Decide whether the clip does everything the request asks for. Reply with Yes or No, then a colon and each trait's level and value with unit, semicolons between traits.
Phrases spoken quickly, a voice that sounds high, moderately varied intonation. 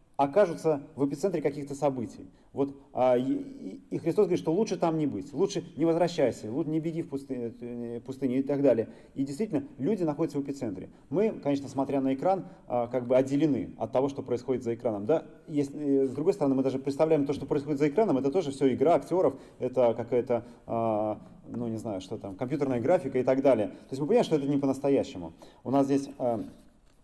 No: fast, 195 wpm; medium, 140 Hz; average, 3.7 semitones